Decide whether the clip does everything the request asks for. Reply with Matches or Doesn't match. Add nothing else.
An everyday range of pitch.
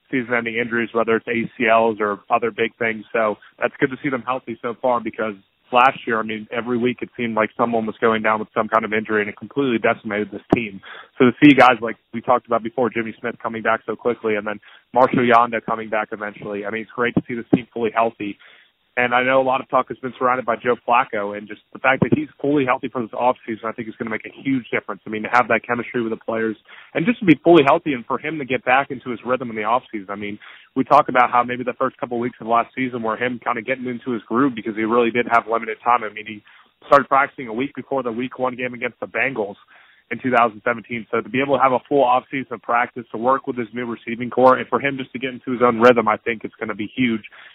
Doesn't match